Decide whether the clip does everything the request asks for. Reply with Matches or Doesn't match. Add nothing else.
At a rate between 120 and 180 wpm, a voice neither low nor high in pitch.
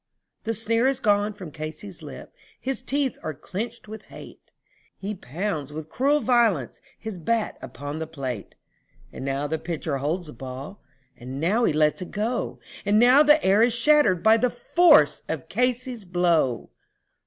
Doesn't match